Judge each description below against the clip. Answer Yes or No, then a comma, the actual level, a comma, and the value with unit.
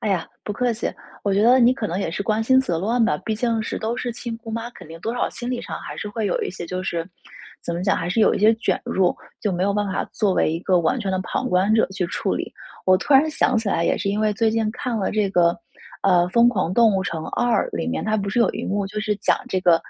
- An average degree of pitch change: Yes, average, 3.6 semitones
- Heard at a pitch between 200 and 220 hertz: Yes, high, 210 Hz